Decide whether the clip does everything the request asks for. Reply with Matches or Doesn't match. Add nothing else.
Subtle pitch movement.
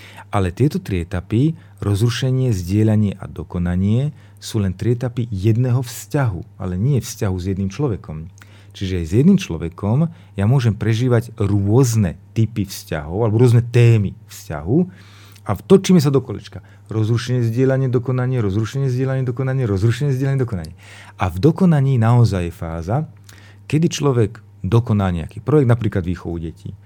Doesn't match